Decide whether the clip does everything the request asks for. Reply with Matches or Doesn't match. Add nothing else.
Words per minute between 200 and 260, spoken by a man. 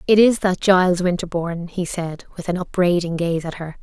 Doesn't match